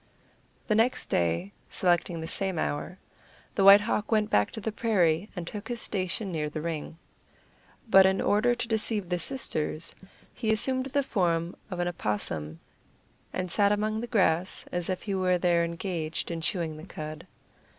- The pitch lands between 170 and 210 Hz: Yes, medium, 185 Hz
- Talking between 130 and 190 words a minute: Yes, average, 170 wpm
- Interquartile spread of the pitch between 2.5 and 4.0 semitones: No, average, 4.4 semitones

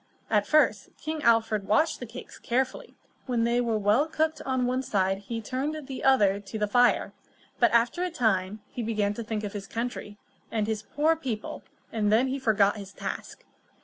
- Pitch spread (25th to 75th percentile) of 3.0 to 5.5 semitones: Yes, average, 3.9 semitones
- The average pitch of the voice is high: Yes, high, 230 Hz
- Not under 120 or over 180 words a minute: No, average, 195 wpm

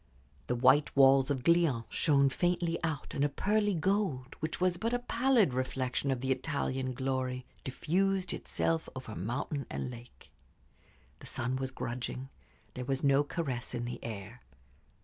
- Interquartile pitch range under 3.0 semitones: No, average, 4.7 semitones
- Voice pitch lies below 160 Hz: Yes, low, 135 Hz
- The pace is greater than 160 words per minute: No, average, 155 wpm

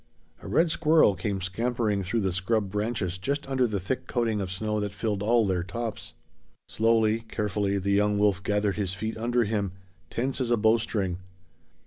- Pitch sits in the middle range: No, low, 105 Hz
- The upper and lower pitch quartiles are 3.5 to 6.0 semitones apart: No, average, 2.9 semitones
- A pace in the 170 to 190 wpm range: Yes, average, 175 wpm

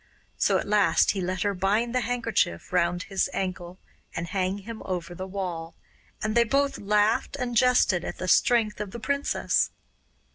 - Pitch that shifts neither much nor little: Yes, average, 4.2 semitones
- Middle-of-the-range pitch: No, high, 200 Hz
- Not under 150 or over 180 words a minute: Yes, average, 175 wpm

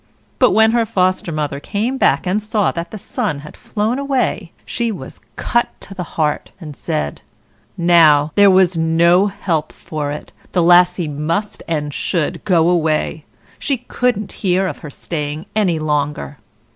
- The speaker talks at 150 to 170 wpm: Yes, average, 160 wpm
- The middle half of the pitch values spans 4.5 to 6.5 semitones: Yes, average, 5.1 semitones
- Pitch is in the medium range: Yes, medium, 175 Hz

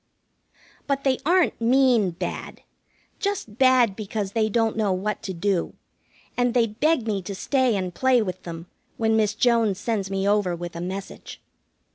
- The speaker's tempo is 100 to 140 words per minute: No, average, 165 wpm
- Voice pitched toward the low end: No, high, 215 Hz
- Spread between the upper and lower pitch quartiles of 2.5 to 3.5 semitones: No, average, 4.2 semitones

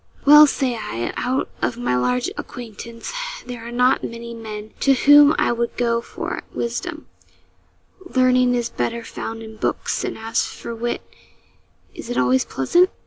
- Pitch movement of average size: No, narrow, 2.2 semitones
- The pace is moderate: Yes, average, 155 wpm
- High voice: Yes, high, 235 Hz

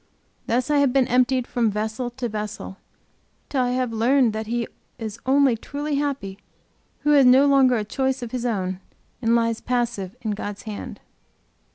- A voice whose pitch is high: Yes, high, 240 Hz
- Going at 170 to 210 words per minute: Yes, average, 175 wpm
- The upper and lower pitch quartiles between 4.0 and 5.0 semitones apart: No, average, 3.3 semitones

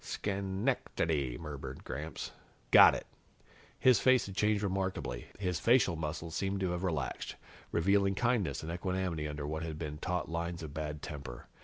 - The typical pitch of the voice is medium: No, very low, 85 Hz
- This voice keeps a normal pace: Yes, average, 170 wpm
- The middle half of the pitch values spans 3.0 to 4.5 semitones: Yes, average, 4.2 semitones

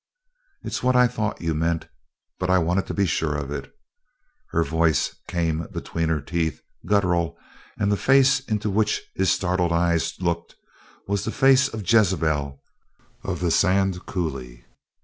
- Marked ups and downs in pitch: No, average, 3.9 semitones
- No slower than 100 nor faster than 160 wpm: Yes, average, 155 wpm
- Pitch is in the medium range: No, very low, 90 Hz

